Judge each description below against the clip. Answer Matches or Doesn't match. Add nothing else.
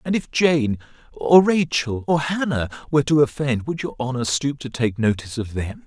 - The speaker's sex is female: Doesn't match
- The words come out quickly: Doesn't match